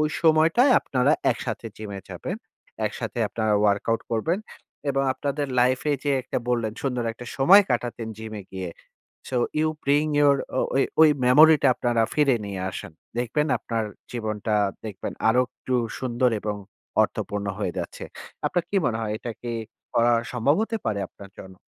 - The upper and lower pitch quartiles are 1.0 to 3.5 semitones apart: No, average, 4.6 semitones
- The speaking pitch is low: Yes, low, 120 Hz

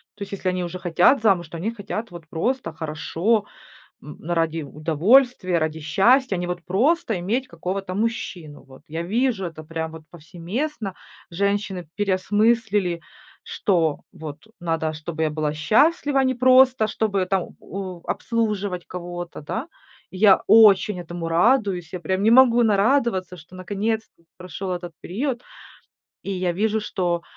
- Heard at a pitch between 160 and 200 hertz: Yes, medium, 185 Hz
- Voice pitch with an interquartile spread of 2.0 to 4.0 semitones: No, average, 4.5 semitones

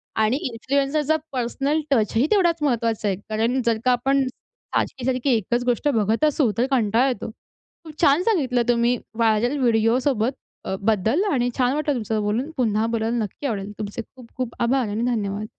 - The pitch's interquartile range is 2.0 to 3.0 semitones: No, average, 3.5 semitones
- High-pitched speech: Yes, high, 240 Hz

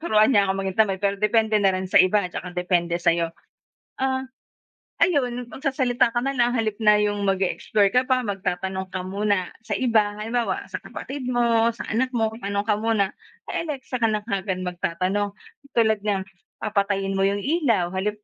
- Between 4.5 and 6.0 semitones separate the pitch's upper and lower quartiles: No, average, 3.6 semitones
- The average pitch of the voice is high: Yes, high, 210 Hz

